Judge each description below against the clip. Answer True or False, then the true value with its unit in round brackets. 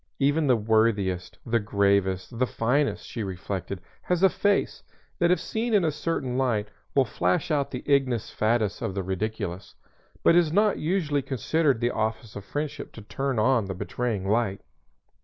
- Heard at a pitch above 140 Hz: False (120 Hz)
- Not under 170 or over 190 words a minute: True (175 wpm)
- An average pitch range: False (6.2 semitones)